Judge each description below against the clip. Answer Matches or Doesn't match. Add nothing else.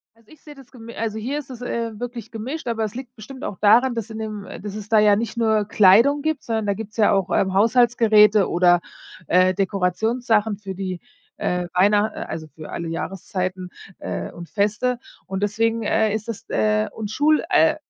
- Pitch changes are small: Doesn't match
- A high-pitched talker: Matches